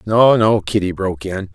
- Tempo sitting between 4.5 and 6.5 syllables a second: Yes, 5.0 syllables/s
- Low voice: Yes, low, 105 Hz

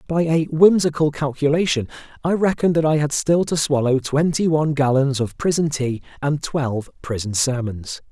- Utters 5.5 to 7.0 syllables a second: No, 5.1 syllables/s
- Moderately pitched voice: Yes, medium, 145 Hz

